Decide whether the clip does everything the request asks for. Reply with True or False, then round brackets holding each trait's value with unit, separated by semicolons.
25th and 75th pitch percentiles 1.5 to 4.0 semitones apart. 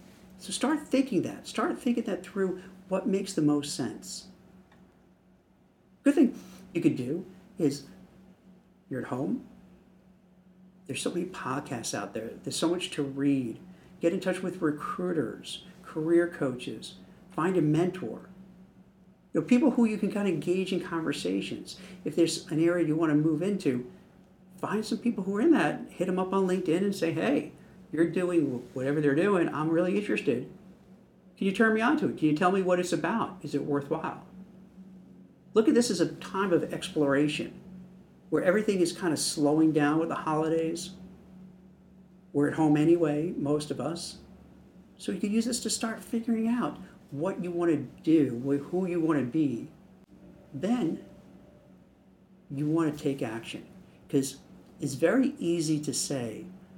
True (3.6 semitones)